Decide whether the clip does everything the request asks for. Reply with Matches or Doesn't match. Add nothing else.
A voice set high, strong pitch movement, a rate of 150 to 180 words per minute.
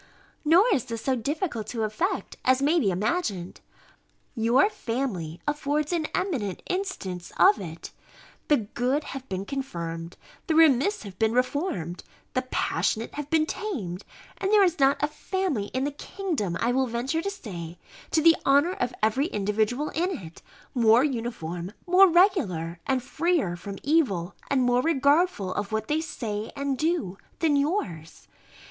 Matches